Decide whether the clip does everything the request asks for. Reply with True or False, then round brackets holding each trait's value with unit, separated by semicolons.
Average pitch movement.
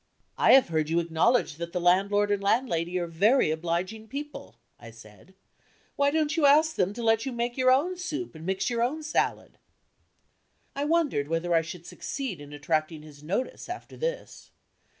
False (8.7 semitones)